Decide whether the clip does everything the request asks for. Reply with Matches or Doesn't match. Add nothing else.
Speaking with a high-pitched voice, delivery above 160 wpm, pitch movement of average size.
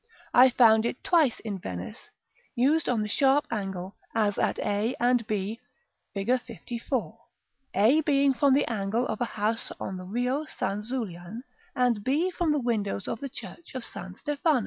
Matches